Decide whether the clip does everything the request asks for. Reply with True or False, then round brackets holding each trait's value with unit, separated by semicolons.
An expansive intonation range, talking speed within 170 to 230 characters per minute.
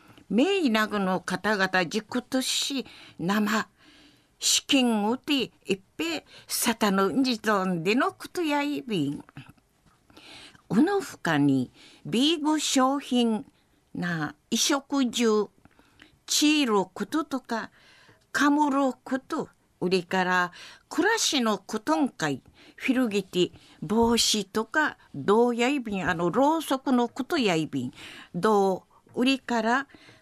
True (6.0 semitones; 220 characters per minute)